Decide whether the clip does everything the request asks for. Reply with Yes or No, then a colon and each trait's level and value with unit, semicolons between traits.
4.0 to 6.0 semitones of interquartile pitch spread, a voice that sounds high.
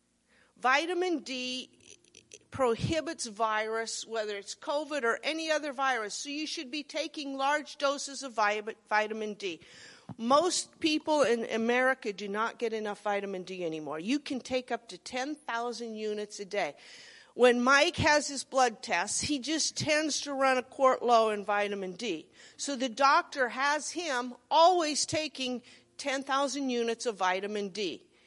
Yes: average, 4.6 semitones; very high, 255 Hz